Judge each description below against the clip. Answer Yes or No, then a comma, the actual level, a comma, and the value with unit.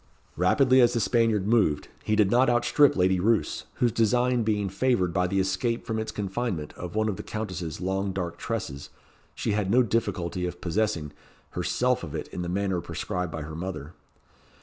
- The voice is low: Yes, low, 100 Hz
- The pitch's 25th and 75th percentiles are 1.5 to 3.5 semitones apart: No, average, 4.2 semitones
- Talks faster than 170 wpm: Yes, average, 185 wpm